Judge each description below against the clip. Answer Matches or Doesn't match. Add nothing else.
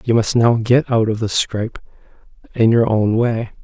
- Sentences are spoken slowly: Doesn't match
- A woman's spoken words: Doesn't match